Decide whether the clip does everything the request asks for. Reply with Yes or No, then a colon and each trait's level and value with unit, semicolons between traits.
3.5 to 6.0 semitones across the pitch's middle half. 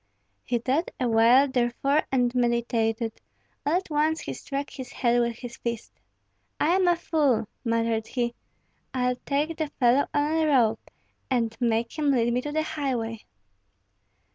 Yes: average, 3.8 semitones